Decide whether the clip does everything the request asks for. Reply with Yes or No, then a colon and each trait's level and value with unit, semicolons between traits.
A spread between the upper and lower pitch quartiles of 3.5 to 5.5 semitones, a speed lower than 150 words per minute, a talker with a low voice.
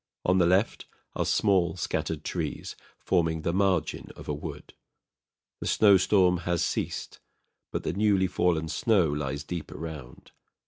No: average, 3.0 semitones; average, 140 wpm; very low, 85 Hz